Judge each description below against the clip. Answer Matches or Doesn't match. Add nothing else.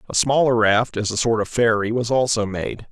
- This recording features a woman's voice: Doesn't match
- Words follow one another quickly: Matches